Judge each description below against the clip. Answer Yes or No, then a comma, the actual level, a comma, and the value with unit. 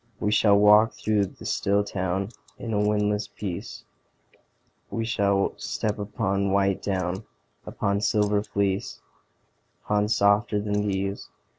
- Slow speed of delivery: Yes, slow, 125 wpm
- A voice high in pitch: No, low, 100 Hz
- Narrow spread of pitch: Yes, narrow, 1.0 semitones